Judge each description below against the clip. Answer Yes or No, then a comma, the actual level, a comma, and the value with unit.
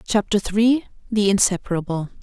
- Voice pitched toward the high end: Yes, high, 205 Hz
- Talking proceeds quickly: No, slow, 80 wpm